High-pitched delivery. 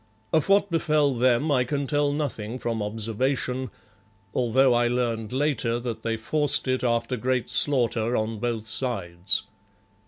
No: low, 125 Hz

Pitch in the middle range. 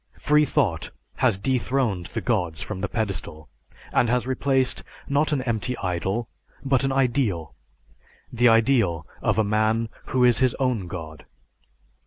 No: low, 115 Hz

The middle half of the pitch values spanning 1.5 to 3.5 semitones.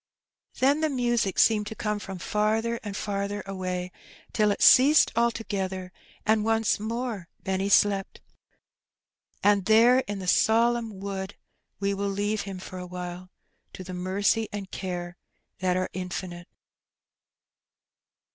Yes: average, 3.0 semitones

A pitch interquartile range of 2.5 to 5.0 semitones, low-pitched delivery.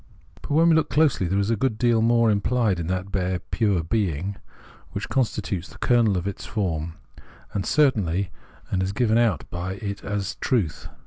Yes: average, 4.1 semitones; low, 100 Hz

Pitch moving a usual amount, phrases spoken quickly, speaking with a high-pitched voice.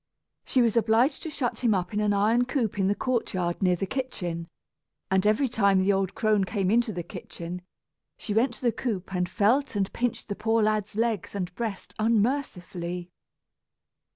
No: average, 3.8 semitones; average, 180 wpm; high, 210 Hz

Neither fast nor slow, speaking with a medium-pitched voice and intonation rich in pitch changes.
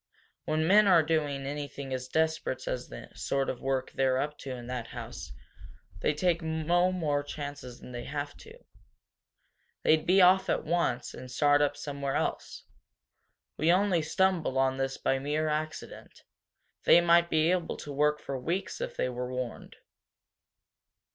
No: average, 160 wpm; medium, 150 Hz; average, 3.9 semitones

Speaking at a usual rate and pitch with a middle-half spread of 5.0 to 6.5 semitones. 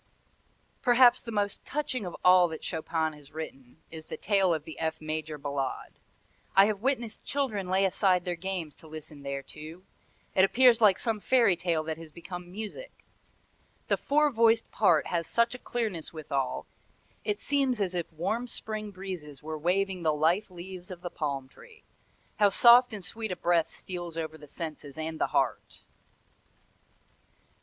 Yes: average, 165 wpm; average, 5.3 semitones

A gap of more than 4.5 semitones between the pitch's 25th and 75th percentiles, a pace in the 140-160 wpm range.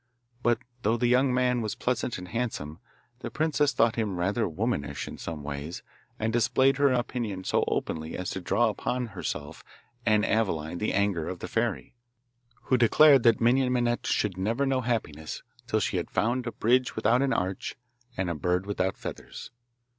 No: average, 5.2 semitones; average, 175 wpm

